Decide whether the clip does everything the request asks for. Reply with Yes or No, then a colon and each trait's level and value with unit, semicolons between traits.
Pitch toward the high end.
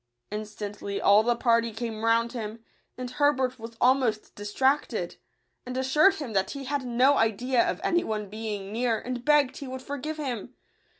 Yes: high, 240 Hz